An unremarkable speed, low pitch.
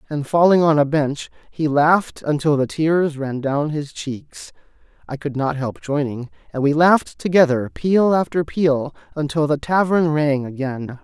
No: average, 170 wpm; medium, 150 Hz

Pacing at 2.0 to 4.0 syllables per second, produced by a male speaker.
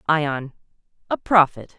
Yes: 3.7 syllables/s; male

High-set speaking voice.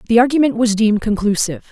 Yes: high, 220 Hz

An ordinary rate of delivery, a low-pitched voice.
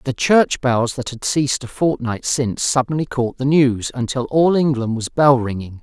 Yes: average, 195 wpm; low, 130 Hz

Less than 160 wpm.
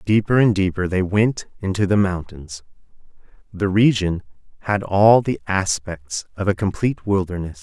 Yes: average, 140 wpm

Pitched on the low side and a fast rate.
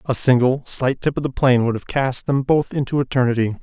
Yes: low, 130 Hz; fast, 230 wpm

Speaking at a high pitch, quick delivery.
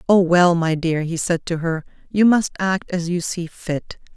No: medium, 175 Hz; fast, 215 wpm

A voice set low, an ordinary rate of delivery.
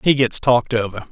No: low, 120 Hz; fast, 215 wpm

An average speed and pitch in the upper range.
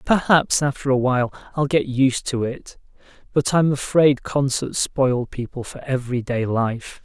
No: average, 155 wpm; low, 130 Hz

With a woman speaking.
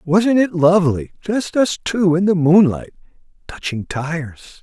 No: male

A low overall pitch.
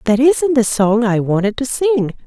No: high, 240 Hz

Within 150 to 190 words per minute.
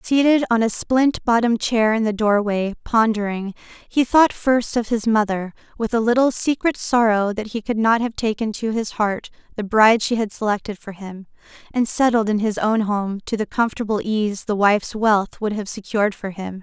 No: average, 200 wpm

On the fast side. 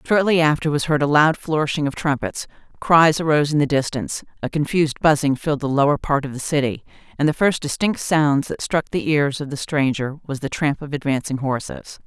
Yes: fast, 210 wpm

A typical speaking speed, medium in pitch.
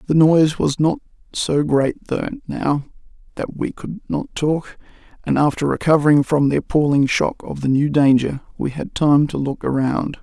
Yes: average, 175 wpm; medium, 145 Hz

